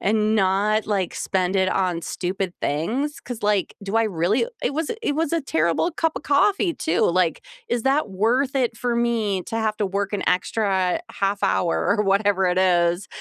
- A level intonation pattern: No, average, 4.3 semitones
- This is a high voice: Yes, high, 205 Hz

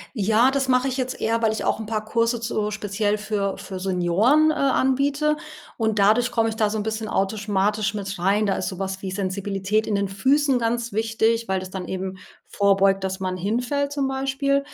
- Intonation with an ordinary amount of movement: Yes, average, 3.8 semitones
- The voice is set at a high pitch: Yes, high, 215 Hz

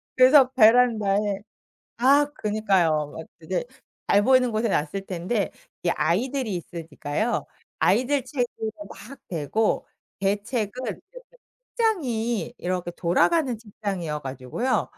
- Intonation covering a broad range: Yes, wide, 5.9 semitones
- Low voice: No, high, 210 Hz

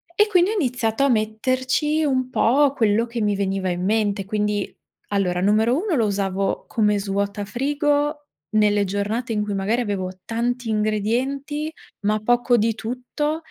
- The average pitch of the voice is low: No, high, 225 Hz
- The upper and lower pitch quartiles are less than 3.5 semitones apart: No, average, 4.1 semitones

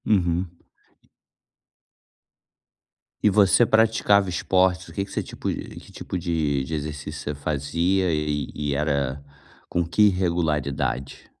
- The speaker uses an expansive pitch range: No, average, 4.2 semitones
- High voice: No, very low, 85 Hz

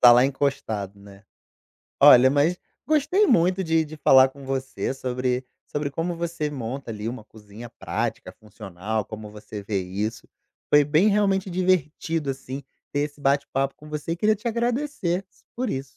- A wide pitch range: Yes, wide, 6.4 semitones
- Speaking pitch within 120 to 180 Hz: Yes, medium, 140 Hz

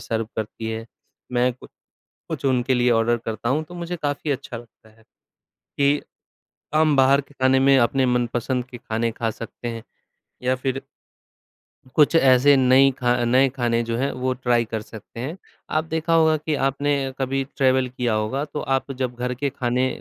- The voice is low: Yes, low, 130 Hz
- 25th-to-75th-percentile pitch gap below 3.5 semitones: Yes, average, 2.7 semitones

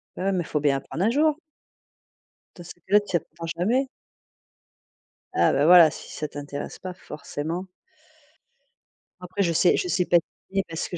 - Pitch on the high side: No, medium, 175 Hz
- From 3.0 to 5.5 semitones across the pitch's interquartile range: Yes, average, 3.5 semitones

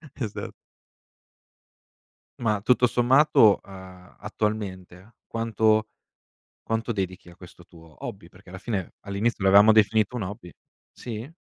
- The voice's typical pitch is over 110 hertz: No, low, 105 Hz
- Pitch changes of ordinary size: Yes, average, 3.4 semitones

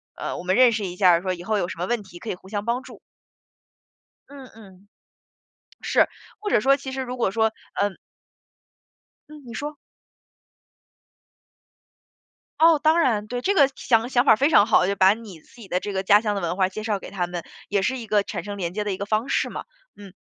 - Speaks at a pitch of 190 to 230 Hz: Yes, high, 210 Hz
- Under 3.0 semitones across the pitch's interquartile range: No, average, 4.6 semitones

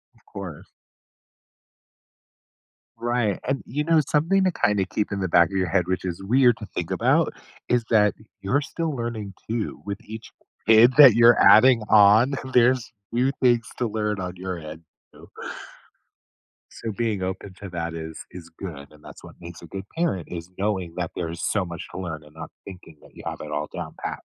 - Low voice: Yes, low, 100 Hz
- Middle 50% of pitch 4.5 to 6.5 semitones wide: Yes, average, 5.3 semitones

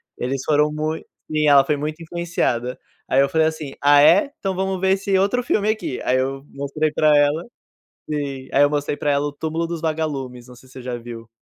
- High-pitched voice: No, medium, 150 Hz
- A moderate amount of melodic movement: Yes, average, 3.0 semitones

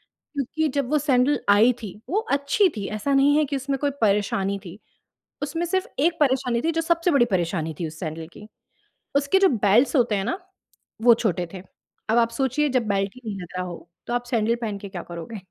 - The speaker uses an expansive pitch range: Yes, wide, 6.4 semitones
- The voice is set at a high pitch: Yes, high, 235 Hz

